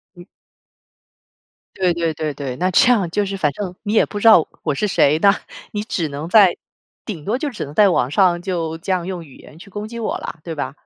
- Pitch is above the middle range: No, medium, 180 Hz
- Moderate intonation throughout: Yes, average, 4.4 semitones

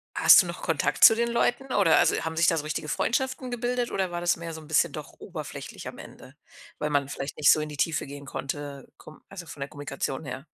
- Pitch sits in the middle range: Yes, medium, 160 Hz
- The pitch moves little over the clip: No, wide, 5.6 semitones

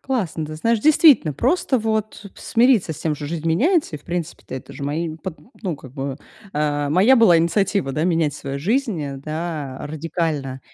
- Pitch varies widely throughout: Yes, wide, 6.3 semitones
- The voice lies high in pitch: No, medium, 165 Hz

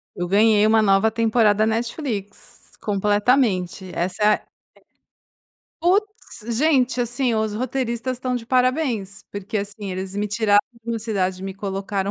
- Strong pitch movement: No, average, 3.4 semitones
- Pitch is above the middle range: Yes, high, 215 Hz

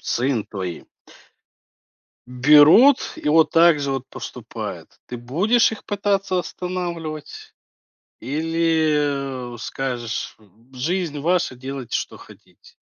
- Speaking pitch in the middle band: Yes, medium, 150 Hz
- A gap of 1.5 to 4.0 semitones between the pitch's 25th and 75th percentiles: No, average, 5.1 semitones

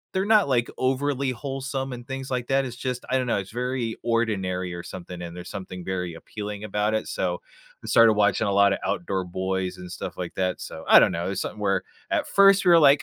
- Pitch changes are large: Yes, wide, 6.0 semitones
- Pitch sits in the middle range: No, low, 110 Hz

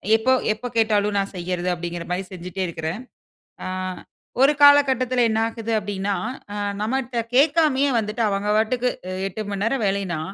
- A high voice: Yes, high, 215 Hz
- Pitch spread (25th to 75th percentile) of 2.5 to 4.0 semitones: No, average, 4.7 semitones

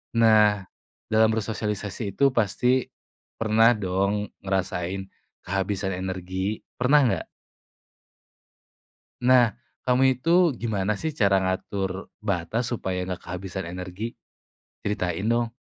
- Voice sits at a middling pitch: No, low, 100 Hz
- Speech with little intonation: No, average, 3.2 semitones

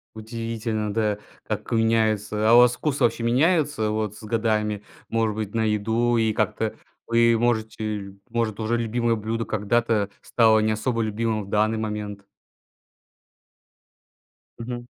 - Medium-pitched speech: No, low, 110 Hz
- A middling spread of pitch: No, narrow, 1.5 semitones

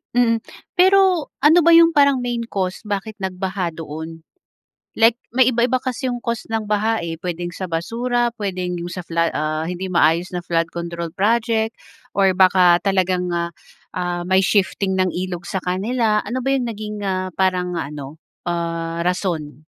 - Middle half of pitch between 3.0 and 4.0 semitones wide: No, average, 4.9 semitones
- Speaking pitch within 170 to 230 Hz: Yes, medium, 185 Hz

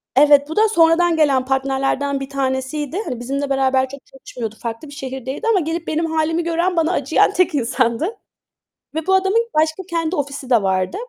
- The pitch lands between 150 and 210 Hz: No, very high, 285 Hz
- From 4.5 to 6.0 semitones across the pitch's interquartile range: No, average, 3.9 semitones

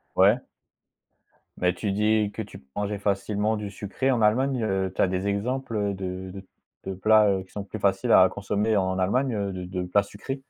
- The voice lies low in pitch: Yes, low, 100 Hz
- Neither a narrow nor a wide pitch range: No, narrow, 2.3 semitones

